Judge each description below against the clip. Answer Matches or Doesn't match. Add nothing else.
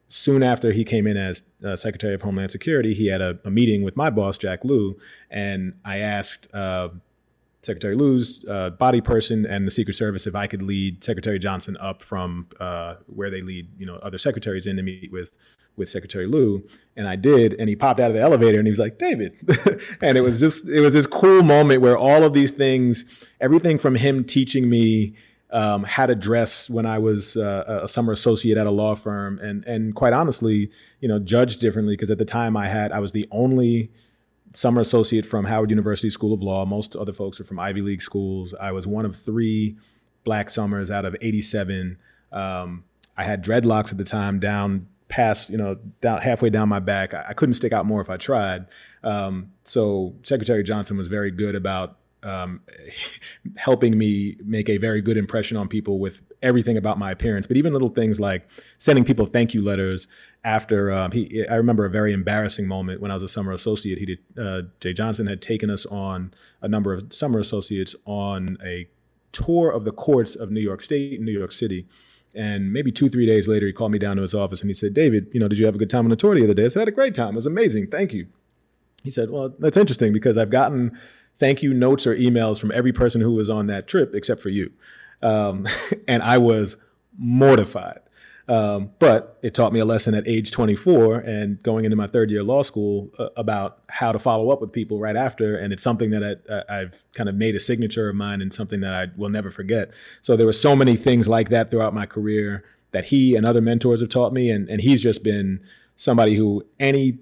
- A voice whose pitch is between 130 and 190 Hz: Doesn't match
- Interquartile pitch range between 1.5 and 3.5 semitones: Matches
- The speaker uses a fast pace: Matches